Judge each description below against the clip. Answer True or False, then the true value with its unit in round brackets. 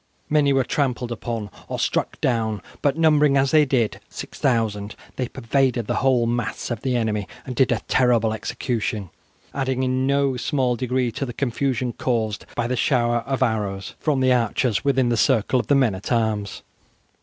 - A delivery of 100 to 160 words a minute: False (175 wpm)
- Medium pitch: False (125 Hz)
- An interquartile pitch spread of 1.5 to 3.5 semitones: True (2.8 semitones)